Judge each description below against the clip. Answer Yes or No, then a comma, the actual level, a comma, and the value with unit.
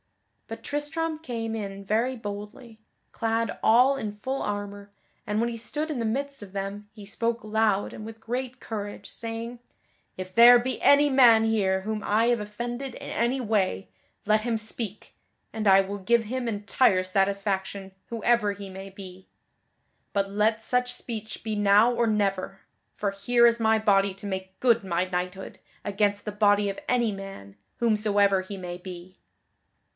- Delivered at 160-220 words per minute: Yes, average, 165 wpm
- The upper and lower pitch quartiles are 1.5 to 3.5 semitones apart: Yes, average, 3.0 semitones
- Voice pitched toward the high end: Yes, high, 215 Hz